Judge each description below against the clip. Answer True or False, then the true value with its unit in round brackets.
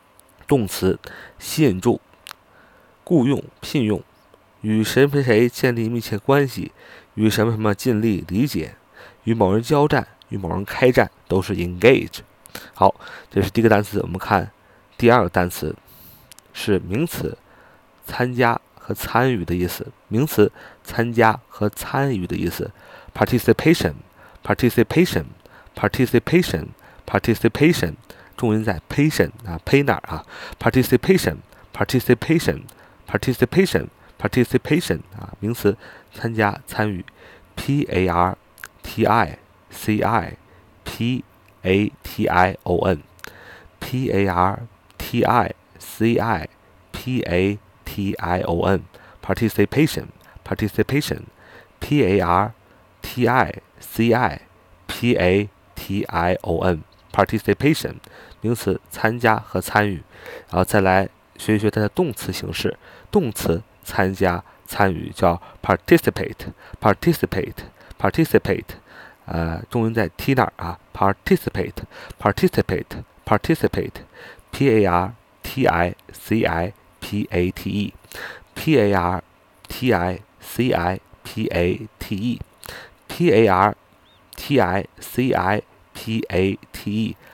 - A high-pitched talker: False (105 Hz)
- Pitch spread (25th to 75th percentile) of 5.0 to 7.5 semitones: False (4.0 semitones)